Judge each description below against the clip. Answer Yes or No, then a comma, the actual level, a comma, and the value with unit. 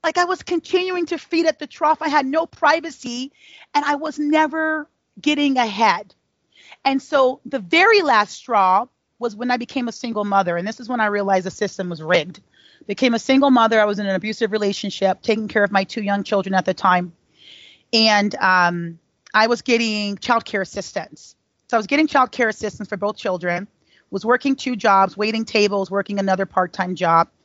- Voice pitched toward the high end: Yes, high, 225 Hz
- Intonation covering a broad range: Yes, wide, 6.0 semitones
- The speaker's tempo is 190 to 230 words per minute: Yes, average, 195 wpm